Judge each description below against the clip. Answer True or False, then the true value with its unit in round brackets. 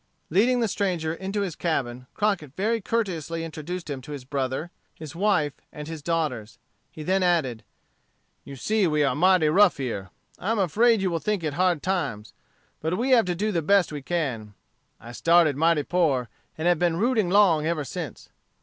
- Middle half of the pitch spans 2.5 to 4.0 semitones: False (4.7 semitones)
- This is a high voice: False (165 Hz)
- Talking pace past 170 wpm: True (185 wpm)